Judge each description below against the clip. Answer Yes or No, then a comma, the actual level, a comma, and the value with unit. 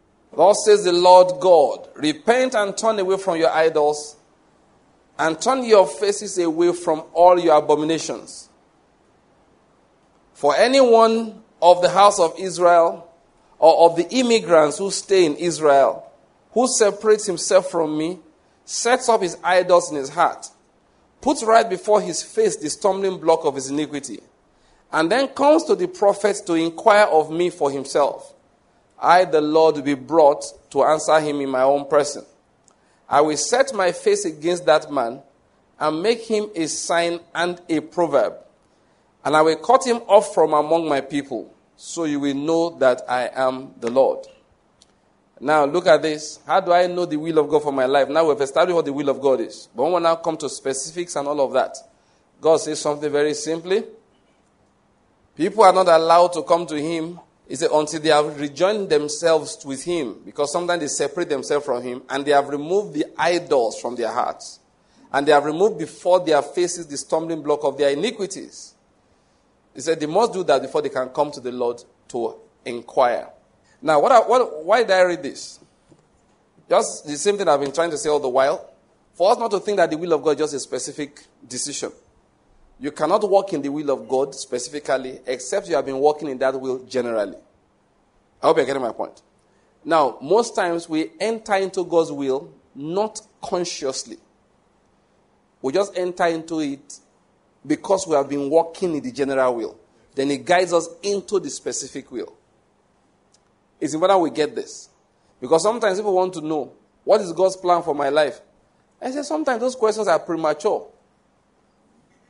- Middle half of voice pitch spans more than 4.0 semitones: Yes, average, 4.5 semitones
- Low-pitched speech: No, medium, 165 Hz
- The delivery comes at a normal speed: Yes, average, 180 wpm